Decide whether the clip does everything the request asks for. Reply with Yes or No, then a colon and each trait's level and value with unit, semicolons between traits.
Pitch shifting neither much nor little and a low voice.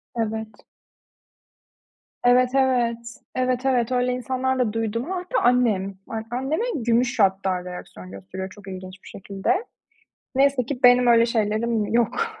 No: average, 3.6 semitones; high, 235 Hz